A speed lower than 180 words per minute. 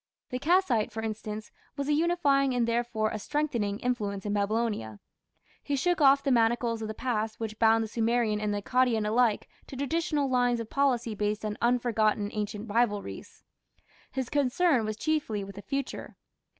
Yes: average, 170 wpm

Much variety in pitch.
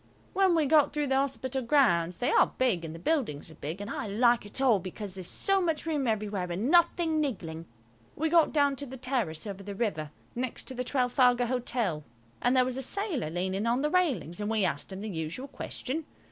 Yes: wide, 7.1 semitones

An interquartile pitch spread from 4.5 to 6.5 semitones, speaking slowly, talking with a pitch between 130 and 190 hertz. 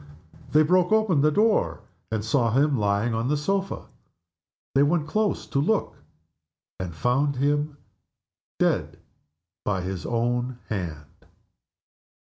Yes: wide, 5.5 semitones; slow, 125 wpm; medium, 140 Hz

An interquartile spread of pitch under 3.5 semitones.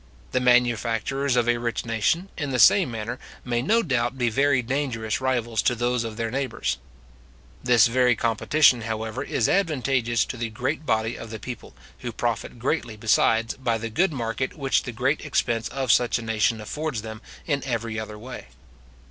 Yes: average, 2.8 semitones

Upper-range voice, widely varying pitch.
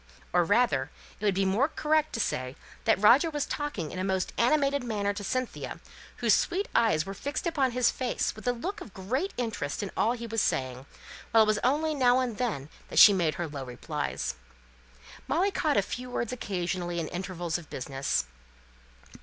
Yes: high, 215 Hz; wide, 6.5 semitones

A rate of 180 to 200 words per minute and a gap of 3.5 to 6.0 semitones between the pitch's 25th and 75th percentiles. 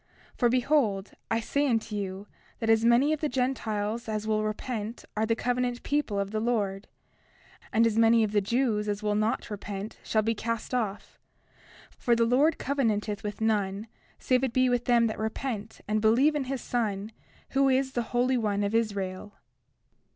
No: average, 185 wpm; average, 3.0 semitones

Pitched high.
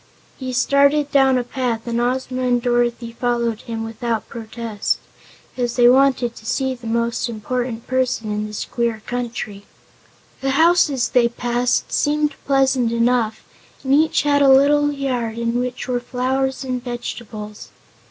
Yes: high, 245 Hz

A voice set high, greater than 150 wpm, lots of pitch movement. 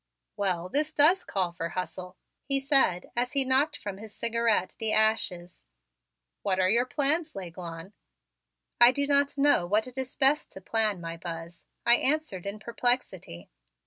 Yes: high, 220 Hz; average, 160 wpm; wide, 6.9 semitones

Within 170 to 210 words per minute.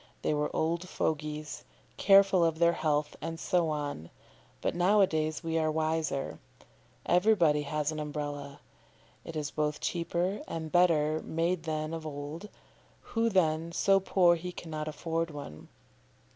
No: average, 145 wpm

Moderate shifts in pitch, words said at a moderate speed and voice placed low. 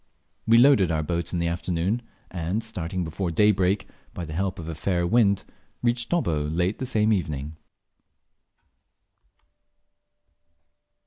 No: average, 4.3 semitones; slow, 130 wpm; very low, 90 Hz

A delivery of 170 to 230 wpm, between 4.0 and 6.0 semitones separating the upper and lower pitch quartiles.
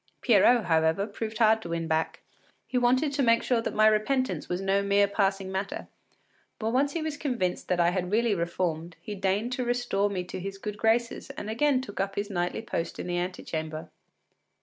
Yes: average, 200 wpm; average, 4.6 semitones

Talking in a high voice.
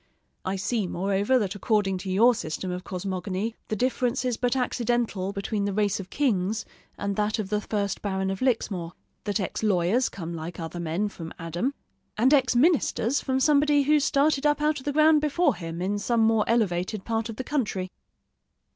Yes: high, 210 Hz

